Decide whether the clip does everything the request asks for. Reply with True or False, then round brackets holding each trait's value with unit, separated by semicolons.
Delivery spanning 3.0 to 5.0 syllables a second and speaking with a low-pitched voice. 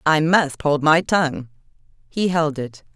False (4.4 syllables/s; 155 Hz)